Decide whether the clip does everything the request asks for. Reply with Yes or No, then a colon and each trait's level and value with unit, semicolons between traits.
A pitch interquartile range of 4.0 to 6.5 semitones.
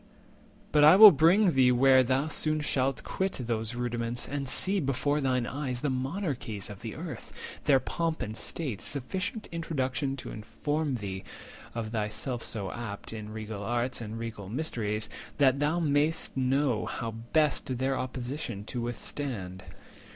Yes: average, 4.5 semitones